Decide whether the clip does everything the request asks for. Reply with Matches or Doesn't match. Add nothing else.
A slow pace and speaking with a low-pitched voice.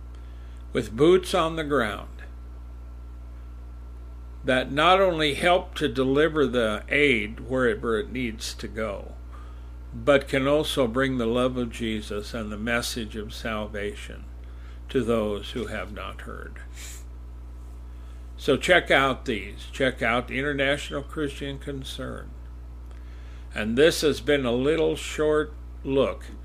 Matches